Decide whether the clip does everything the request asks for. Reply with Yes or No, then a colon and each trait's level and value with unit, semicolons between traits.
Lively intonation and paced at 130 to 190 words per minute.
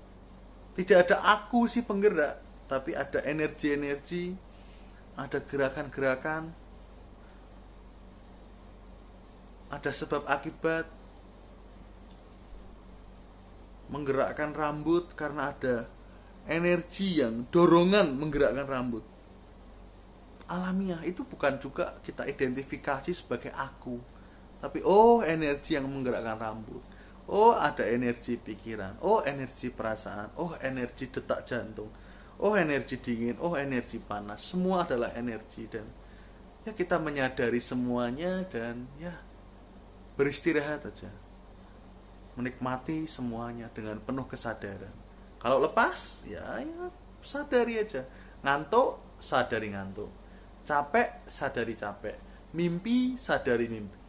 No: wide, 7.1 semitones; average, 95 wpm